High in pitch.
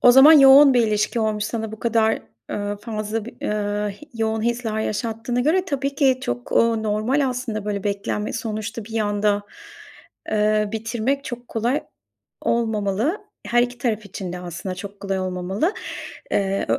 Yes: high, 220 Hz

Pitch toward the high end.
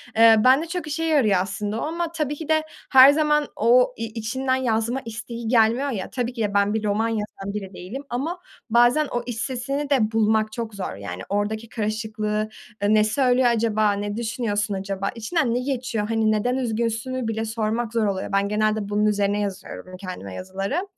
Yes: high, 225 Hz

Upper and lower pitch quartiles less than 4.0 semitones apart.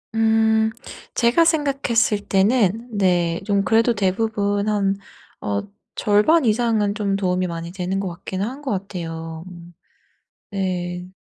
Yes: average, 3.6 semitones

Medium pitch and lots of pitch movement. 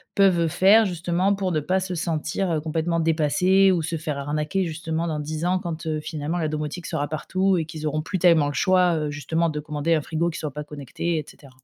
No: medium, 160 Hz; average, 2.7 semitones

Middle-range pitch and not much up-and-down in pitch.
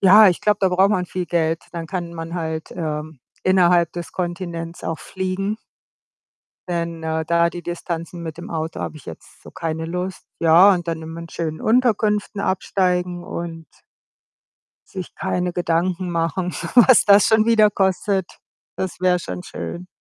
Yes: medium, 175 Hz; narrow, 2.2 semitones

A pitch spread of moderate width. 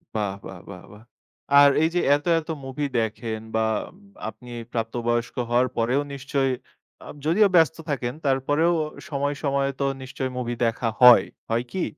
Yes: average, 3.7 semitones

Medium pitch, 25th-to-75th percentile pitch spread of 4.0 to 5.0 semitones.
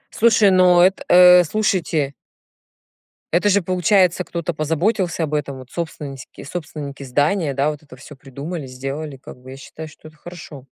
Yes: medium, 155 Hz; average, 4.3 semitones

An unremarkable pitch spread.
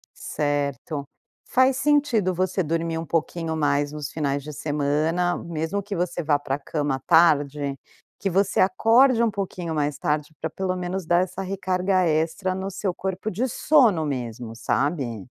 Yes: average, 4.5 semitones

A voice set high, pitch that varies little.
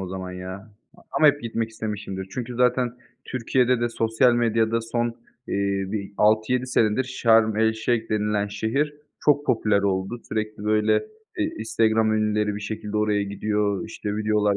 No: low, 110 Hz; narrow, 2.1 semitones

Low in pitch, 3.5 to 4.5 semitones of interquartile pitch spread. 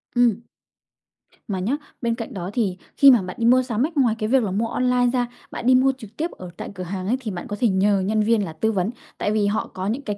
No: high, 220 Hz; average, 4.1 semitones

